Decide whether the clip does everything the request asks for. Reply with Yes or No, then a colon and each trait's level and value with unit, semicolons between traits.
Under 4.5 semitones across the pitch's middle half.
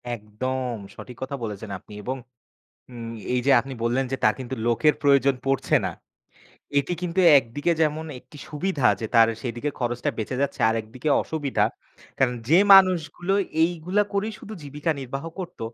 No: average, 4.9 semitones